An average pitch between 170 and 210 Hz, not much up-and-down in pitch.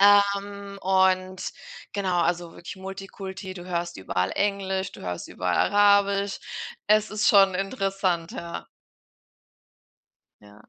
Yes: high, 190 Hz; narrow, 2.2 semitones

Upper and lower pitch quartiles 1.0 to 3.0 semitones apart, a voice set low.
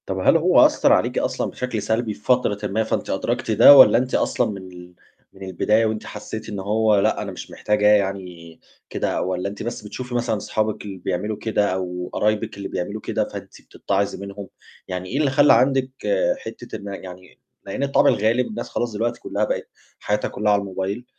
Yes: narrow, 2.6 semitones; low, 105 Hz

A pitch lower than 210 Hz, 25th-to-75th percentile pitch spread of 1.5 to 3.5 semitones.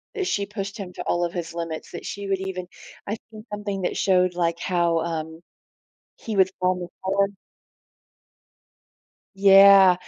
Yes: medium, 185 Hz; narrow, 2.4 semitones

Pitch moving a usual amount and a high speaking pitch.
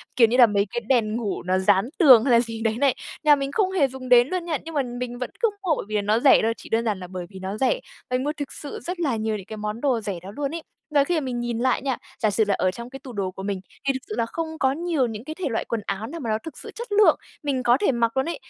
Yes: average, 4.7 semitones; high, 245 Hz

